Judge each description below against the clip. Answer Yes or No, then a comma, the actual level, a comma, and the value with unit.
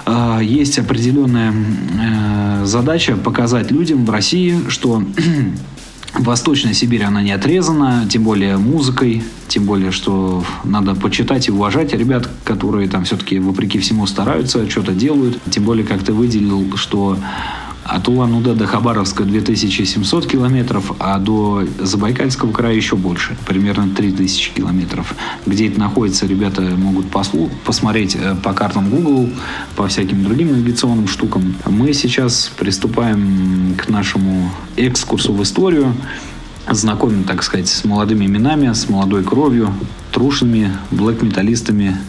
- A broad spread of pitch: No, average, 3.6 semitones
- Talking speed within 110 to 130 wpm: Yes, average, 125 wpm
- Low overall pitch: Yes, low, 105 Hz